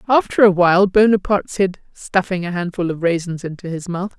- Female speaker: Yes, female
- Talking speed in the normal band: Yes, average, 185 wpm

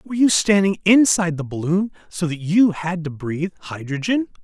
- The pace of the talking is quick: No, average, 175 wpm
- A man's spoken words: Yes, male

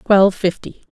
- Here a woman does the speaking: Yes, female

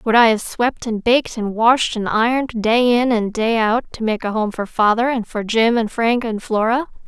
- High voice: Yes, high, 230 Hz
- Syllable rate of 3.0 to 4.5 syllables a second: No, 4.9 syllables/s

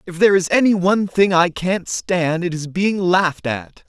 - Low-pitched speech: No, medium, 180 Hz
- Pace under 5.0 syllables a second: Yes, 4.8 syllables/s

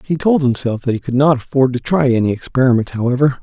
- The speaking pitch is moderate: No, low, 130 Hz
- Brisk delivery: Yes, fast, 230 wpm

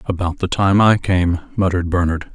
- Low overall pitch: Yes, very low, 90 Hz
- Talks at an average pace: Yes, average, 180 wpm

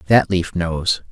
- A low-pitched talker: Yes, very low, 90 Hz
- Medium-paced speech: Yes, average, 160 wpm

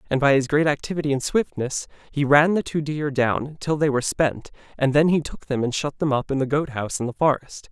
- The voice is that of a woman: No, male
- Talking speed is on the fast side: Yes, fast, 255 wpm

